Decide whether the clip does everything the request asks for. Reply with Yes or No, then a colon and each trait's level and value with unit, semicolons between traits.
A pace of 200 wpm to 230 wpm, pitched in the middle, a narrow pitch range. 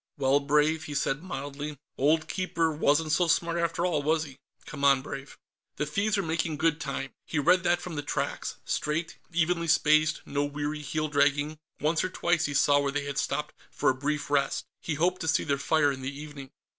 Yes: fast, 205 wpm; medium, 150 Hz; narrow, 2.3 semitones